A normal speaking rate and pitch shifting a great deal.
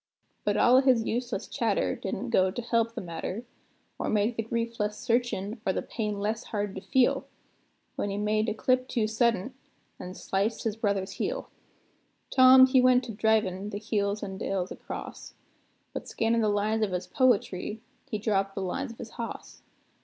No: average, 185 wpm; average, 2.8 semitones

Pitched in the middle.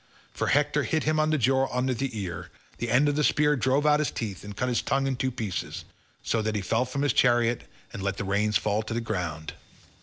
No: low, 125 Hz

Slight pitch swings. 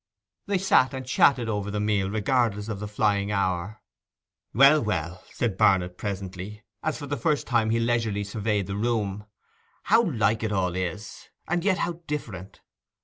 No: average, 4.2 semitones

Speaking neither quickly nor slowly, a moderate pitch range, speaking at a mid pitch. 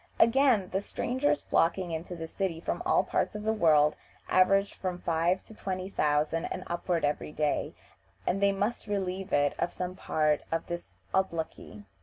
Yes: average, 170 wpm; average, 3.4 semitones; medium, 180 Hz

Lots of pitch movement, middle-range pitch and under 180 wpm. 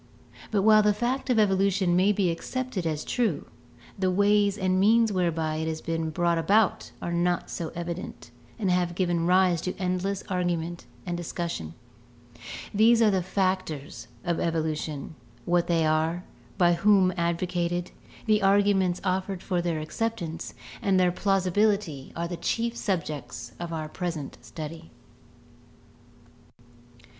No: average, 3.0 semitones; medium, 180 Hz; average, 140 wpm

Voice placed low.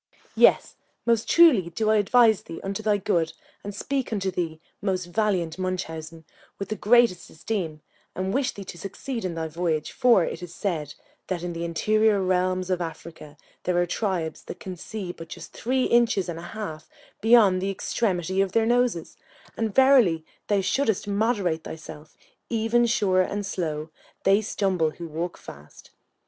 No: medium, 185 Hz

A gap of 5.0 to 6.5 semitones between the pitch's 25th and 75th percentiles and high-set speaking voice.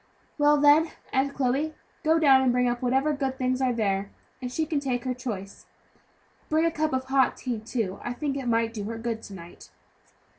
No: average, 3.4 semitones; very high, 255 Hz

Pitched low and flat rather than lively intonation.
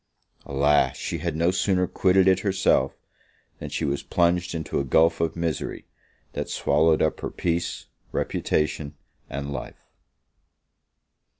No: very low, 80 Hz; average, 3.2 semitones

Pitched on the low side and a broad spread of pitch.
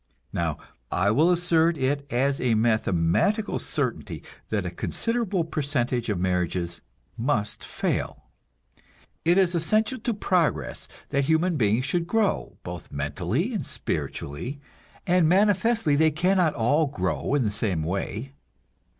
No: medium, 145 Hz; wide, 8.9 semitones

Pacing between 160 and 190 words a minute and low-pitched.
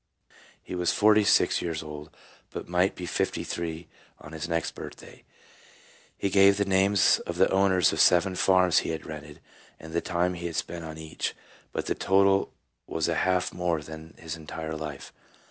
Yes: average, 180 wpm; very low, 85 Hz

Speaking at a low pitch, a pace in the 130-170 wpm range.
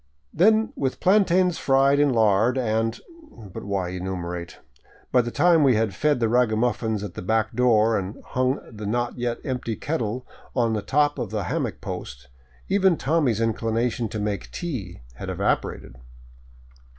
Yes: low, 115 Hz; average, 160 wpm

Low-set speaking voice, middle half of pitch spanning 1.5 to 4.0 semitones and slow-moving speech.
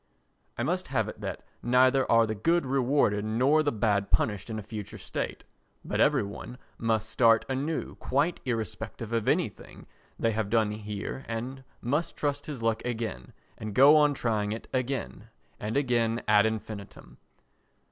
No: low, 115 Hz; average, 3.6 semitones; average, 160 wpm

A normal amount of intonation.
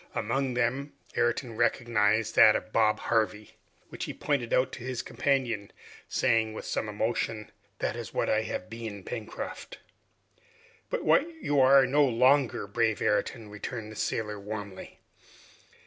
Yes: average, 3.0 semitones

